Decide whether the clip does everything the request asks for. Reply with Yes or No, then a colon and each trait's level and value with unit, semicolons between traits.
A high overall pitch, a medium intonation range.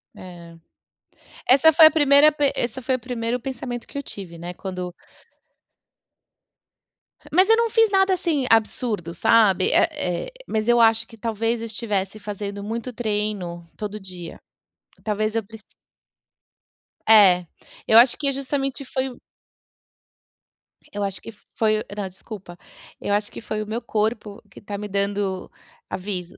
Yes: high, 220 Hz; average, 4.3 semitones